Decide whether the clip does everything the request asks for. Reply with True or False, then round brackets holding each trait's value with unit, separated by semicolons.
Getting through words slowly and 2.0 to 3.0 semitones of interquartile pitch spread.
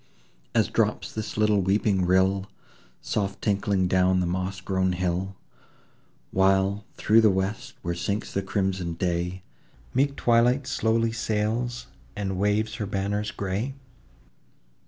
True (125 wpm; 2.6 semitones)